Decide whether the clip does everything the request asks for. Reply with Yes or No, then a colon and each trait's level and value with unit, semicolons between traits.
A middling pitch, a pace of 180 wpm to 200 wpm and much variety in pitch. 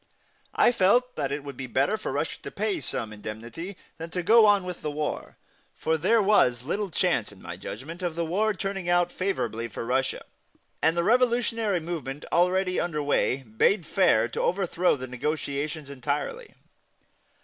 No: medium, 170 Hz; average, 170 wpm; wide, 6.4 semitones